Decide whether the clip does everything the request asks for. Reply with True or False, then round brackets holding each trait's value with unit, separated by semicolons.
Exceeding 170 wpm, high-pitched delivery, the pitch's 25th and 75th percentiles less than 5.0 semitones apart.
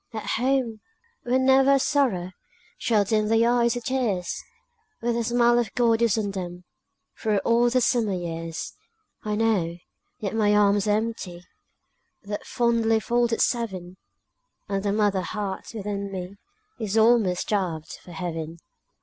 False (150 wpm; 215 Hz; 3.6 semitones)